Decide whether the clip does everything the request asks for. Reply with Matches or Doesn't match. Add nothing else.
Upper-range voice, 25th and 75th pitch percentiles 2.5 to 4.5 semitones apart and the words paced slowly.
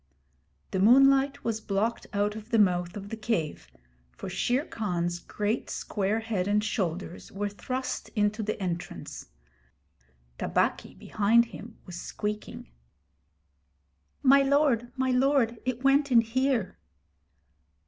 Matches